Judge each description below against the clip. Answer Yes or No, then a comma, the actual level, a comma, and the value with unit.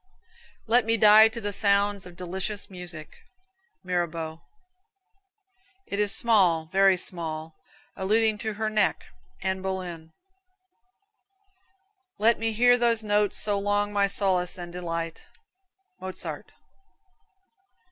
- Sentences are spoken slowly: Yes, slow, 110 wpm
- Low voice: No, high, 195 Hz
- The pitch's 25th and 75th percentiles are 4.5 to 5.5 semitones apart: No, average, 3.1 semitones